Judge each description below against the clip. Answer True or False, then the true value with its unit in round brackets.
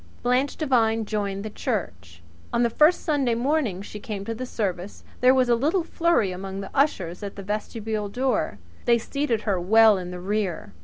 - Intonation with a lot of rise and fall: False (4.4 semitones)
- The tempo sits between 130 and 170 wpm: False (190 wpm)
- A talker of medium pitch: False (220 Hz)